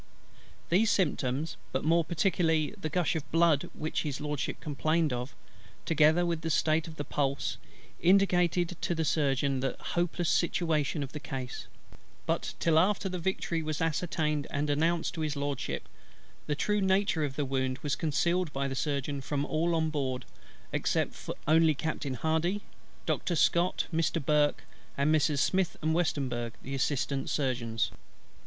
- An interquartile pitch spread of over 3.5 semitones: No, average, 3.1 semitones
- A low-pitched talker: No, medium, 155 Hz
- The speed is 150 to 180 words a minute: Yes, average, 155 wpm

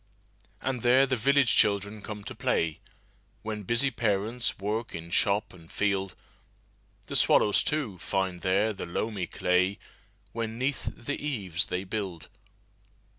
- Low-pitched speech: Yes, low, 105 Hz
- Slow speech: Yes, slow, 125 wpm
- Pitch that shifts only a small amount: No, average, 3.8 semitones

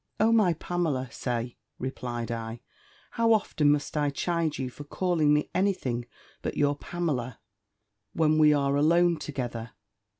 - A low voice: No, medium, 145 Hz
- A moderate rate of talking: Yes, average, 145 wpm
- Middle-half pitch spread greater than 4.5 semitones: Yes, average, 5.2 semitones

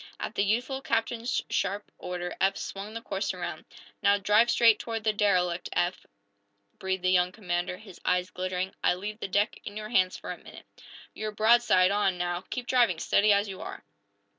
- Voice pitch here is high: Yes, high, 200 Hz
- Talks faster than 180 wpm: Yes, average, 190 wpm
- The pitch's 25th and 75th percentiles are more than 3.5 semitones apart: No, average, 3.0 semitones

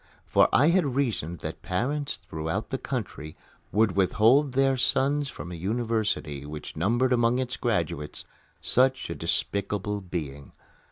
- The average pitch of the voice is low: Yes, low, 110 Hz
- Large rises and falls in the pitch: Yes, wide, 7.2 semitones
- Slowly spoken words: Yes, slow, 130 wpm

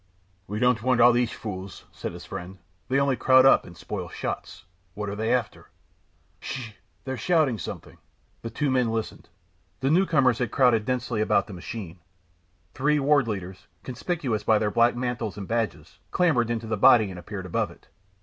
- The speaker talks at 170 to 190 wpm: Yes, average, 180 wpm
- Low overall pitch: Yes, low, 115 Hz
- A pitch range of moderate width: Yes, average, 3.7 semitones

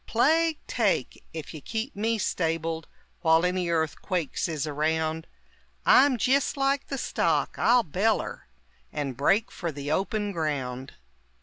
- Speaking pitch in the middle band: Yes, medium, 170 Hz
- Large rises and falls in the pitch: Yes, wide, 6.4 semitones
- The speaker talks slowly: Yes, slow, 130 wpm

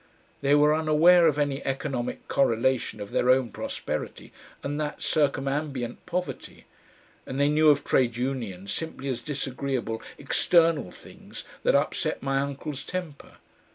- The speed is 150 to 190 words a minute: No, slow, 135 wpm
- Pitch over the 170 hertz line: No, medium, 140 Hz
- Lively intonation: No, average, 2.7 semitones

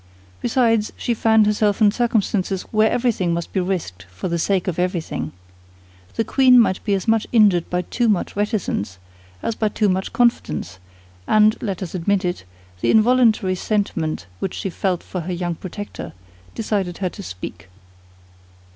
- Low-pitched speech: No, high, 195 Hz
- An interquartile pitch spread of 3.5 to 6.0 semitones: Yes, average, 3.9 semitones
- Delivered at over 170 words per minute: No, average, 155 wpm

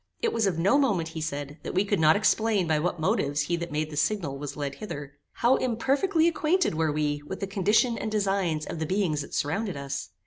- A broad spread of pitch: Yes, wide, 6.1 semitones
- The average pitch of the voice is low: No, medium, 170 Hz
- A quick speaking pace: Yes, fast, 230 wpm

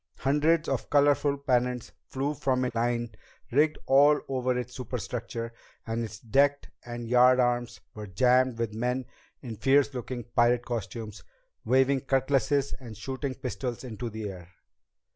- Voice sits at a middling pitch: No, low, 125 Hz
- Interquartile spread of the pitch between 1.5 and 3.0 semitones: Yes, narrow, 2.5 semitones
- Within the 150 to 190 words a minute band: No, slow, 135 wpm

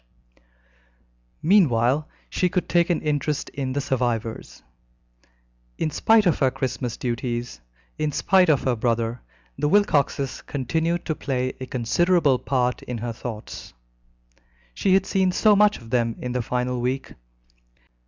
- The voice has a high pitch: No, low, 135 Hz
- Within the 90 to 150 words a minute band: Yes, average, 140 wpm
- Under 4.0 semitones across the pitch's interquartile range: No, average, 5.3 semitones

